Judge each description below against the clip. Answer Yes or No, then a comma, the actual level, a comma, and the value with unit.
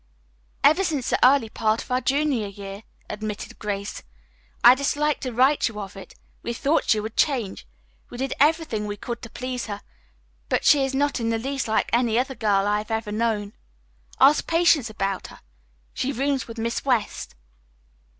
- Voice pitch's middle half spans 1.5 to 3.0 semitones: No, average, 4.4 semitones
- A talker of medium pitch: No, high, 235 Hz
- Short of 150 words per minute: No, average, 180 wpm